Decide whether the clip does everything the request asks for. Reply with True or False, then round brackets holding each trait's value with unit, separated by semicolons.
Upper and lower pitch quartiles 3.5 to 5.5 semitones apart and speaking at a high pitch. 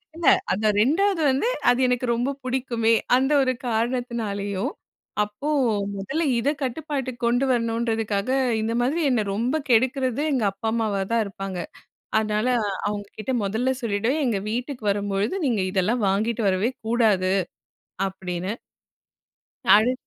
True (3.8 semitones; 230 Hz)